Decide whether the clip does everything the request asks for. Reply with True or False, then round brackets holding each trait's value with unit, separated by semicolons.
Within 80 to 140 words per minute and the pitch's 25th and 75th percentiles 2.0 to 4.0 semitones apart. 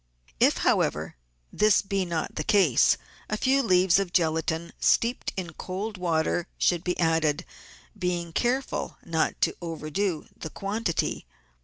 True (135 wpm; 3.6 semitones)